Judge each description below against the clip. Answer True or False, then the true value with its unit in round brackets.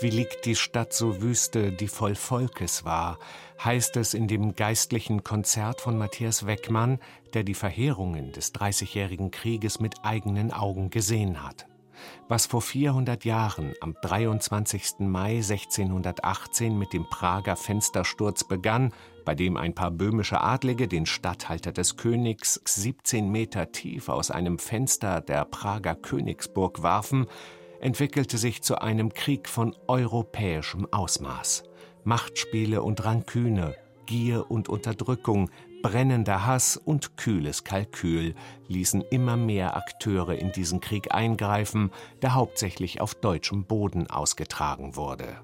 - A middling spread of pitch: True (3.6 semitones)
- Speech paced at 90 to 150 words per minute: True (130 wpm)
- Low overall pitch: True (110 Hz)